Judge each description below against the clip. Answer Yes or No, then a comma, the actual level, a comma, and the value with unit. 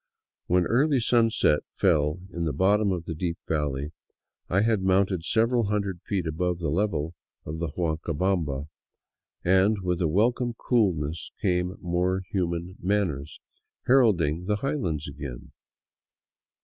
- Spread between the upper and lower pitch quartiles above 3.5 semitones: Yes, average, 4.2 semitones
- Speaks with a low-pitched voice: Yes, very low, 90 Hz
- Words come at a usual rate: No, slow, 130 wpm